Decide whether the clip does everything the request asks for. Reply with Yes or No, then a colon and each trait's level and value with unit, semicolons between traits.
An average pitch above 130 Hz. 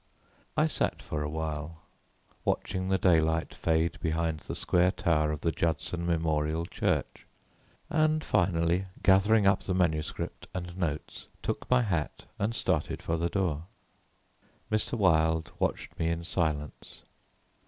No: very low, 85 Hz